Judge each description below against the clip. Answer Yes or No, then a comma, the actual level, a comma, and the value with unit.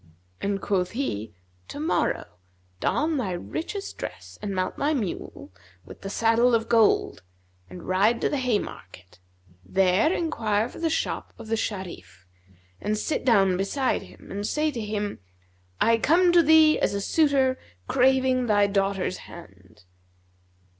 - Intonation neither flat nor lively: No, wide, 5.7 semitones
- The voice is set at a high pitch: Yes, high, 220 Hz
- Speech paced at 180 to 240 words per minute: No, average, 145 wpm